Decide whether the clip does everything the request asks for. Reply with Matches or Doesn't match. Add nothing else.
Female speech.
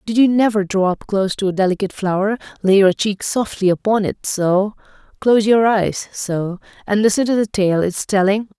Matches